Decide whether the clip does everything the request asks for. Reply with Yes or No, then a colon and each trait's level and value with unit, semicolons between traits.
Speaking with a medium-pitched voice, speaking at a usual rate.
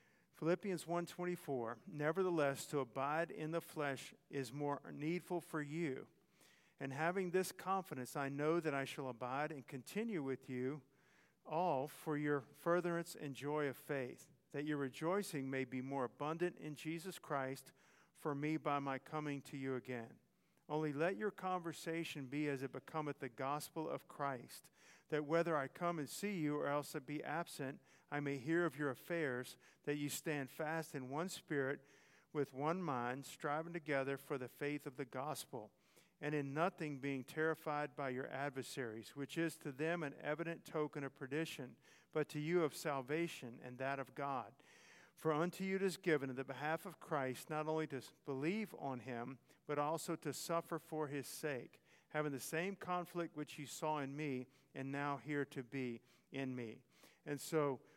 Yes: medium, 150 Hz; average, 175 wpm